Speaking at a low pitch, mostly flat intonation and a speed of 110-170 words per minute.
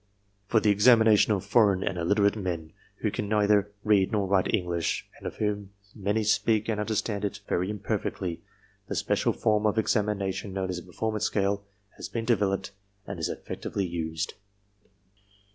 No: low, 100 Hz; narrow, 1.9 semitones; average, 180 wpm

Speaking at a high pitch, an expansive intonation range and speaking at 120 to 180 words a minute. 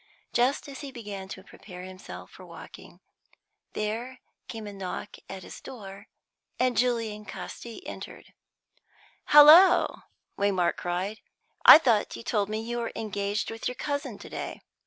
No: high, 220 Hz; average, 3.9 semitones; average, 145 wpm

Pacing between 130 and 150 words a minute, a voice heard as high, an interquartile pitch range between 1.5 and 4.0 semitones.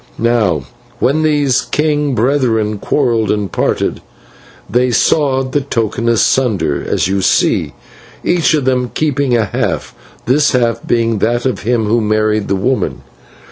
No: average, 140 wpm; low, 120 Hz; average, 3.6 semitones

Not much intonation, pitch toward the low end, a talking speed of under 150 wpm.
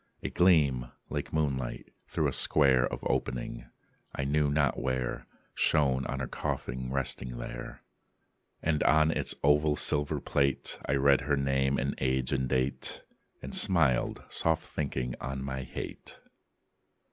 Yes: narrow, 2.3 semitones; very low, 70 Hz; average, 140 wpm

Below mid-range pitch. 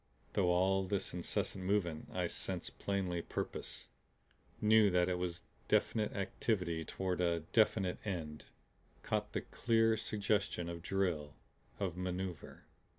Yes: very low, 90 Hz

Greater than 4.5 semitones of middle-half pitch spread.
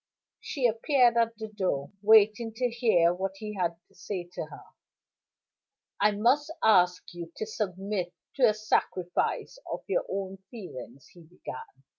No: average, 4.1 semitones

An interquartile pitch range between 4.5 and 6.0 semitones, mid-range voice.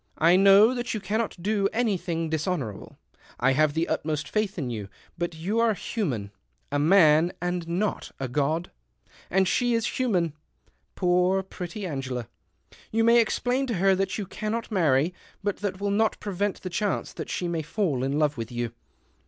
Yes: wide, 5.4 semitones; medium, 180 Hz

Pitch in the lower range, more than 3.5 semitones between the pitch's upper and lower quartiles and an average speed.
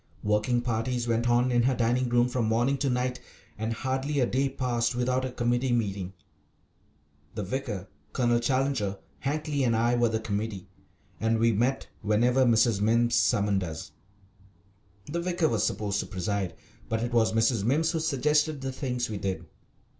No: low, 120 Hz; average, 2.9 semitones; average, 170 wpm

